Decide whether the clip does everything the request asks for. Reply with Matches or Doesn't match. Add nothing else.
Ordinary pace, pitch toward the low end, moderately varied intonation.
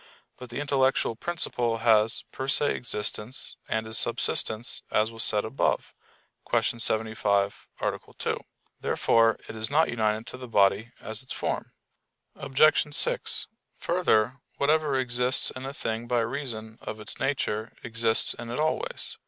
Matches